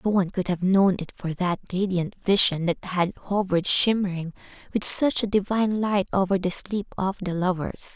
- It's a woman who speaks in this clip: Yes, female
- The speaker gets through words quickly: No, average, 190 wpm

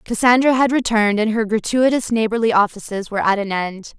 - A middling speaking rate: Yes, average, 180 wpm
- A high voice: Yes, high, 220 Hz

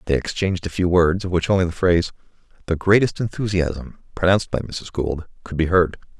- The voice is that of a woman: No, male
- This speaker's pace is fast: No, average, 195 wpm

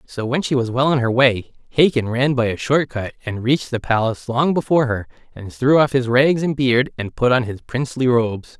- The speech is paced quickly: Yes, fast, 235 wpm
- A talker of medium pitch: No, low, 125 Hz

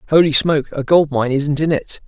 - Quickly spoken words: Yes, fast, 230 wpm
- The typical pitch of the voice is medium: Yes, medium, 145 Hz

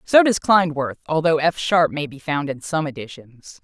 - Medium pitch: Yes, medium, 155 Hz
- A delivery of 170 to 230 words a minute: Yes, average, 200 wpm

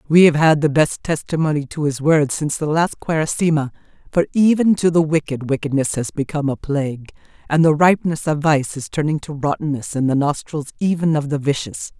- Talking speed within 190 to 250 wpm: Yes, average, 195 wpm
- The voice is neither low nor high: Yes, medium, 150 Hz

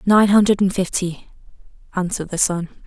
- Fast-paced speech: No, average, 145 wpm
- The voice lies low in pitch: No, high, 190 Hz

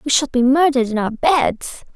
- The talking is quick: Yes, fast, 215 wpm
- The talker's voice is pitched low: No, very high, 265 Hz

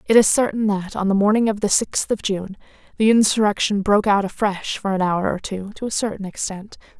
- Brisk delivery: Yes, fast, 225 wpm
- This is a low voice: No, high, 205 Hz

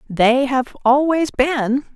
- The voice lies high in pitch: Yes, very high, 265 Hz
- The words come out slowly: Yes, slow, 125 wpm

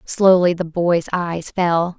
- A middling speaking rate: Yes, average, 150 wpm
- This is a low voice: No, medium, 175 Hz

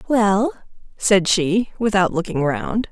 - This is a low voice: No, high, 190 Hz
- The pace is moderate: No, slow, 125 wpm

